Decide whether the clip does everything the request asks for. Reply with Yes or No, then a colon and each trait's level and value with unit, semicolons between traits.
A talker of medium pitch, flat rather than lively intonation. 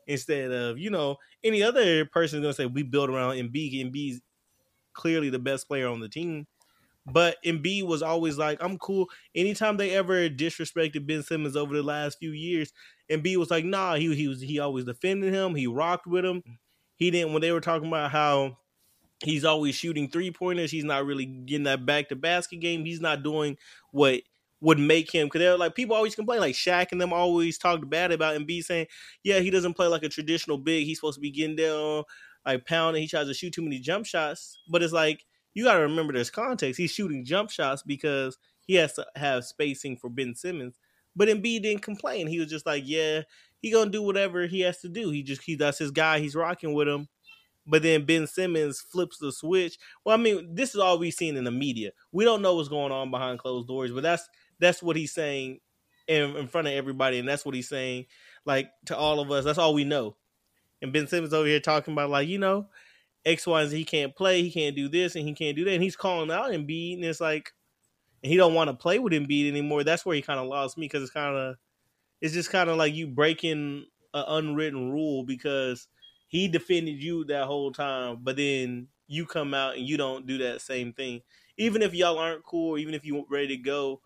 No: medium, 155 Hz; average, 3.3 semitones